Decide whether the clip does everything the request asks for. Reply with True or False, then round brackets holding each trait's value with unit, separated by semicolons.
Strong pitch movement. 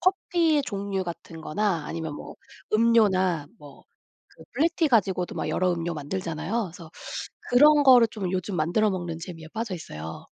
True (5.7 semitones)